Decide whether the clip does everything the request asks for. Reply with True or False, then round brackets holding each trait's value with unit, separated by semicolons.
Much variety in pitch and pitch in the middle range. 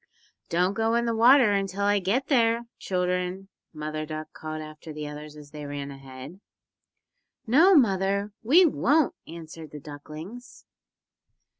True (6.9 semitones; 180 Hz)